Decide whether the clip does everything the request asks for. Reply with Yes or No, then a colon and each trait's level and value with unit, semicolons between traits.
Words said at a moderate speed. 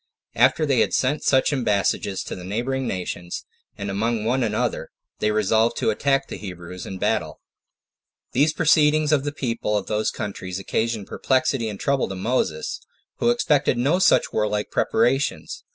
Yes: average, 165 wpm